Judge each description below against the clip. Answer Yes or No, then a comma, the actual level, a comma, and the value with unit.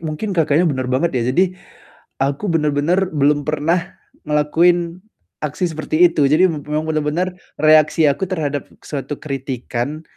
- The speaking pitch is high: No, medium, 155 Hz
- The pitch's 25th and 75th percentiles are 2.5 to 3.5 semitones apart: Yes, average, 2.8 semitones